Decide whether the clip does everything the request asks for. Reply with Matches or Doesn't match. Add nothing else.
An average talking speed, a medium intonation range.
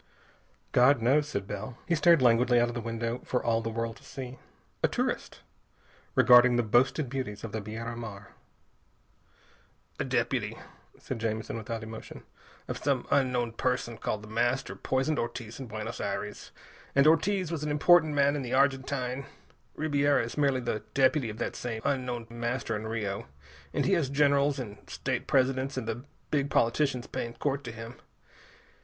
Matches